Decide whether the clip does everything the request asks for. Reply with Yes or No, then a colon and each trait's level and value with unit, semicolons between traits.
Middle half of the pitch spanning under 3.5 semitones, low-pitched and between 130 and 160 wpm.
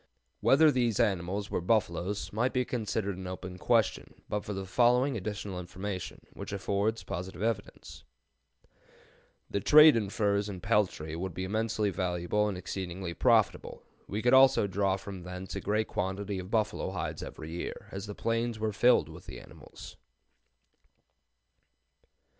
Yes: average, 3.0 semitones; low, 100 Hz; average, 150 wpm